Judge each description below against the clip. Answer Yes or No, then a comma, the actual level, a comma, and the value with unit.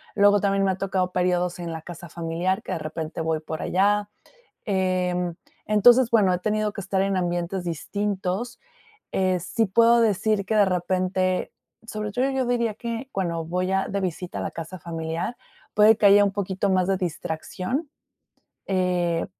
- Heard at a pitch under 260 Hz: Yes, high, 190 Hz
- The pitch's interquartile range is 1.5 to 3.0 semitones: Yes, average, 2.7 semitones